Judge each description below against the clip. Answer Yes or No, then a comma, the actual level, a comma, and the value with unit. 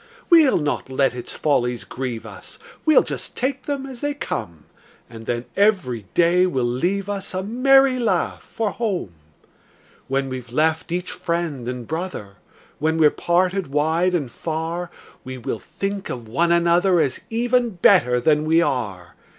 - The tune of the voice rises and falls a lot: Yes, wide, 7.4 semitones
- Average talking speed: Yes, average, 160 wpm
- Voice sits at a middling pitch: Yes, medium, 165 Hz